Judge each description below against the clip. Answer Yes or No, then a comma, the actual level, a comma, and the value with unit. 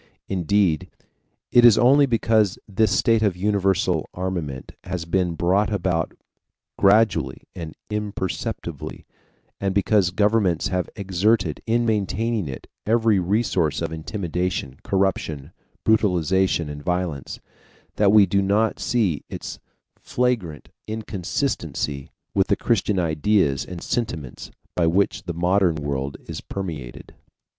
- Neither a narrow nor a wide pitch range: Yes, average, 4.1 semitones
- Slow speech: Yes, slow, 115 wpm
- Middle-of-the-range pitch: No, very low, 95 Hz